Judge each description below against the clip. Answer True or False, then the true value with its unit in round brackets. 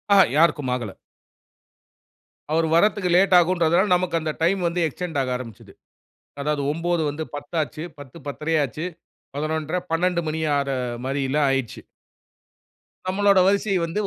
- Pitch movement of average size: True (3.8 semitones)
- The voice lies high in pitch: False (160 Hz)